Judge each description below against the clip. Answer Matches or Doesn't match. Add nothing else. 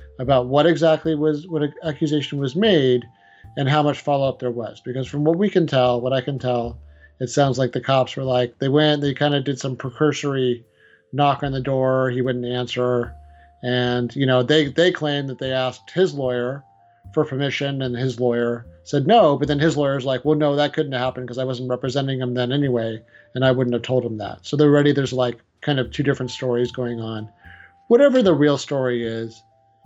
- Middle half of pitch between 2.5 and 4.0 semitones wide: Matches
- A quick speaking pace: Matches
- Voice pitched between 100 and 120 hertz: Doesn't match